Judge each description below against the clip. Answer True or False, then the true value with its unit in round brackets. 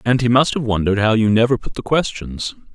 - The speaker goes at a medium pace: False (240 wpm)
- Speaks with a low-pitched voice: True (115 Hz)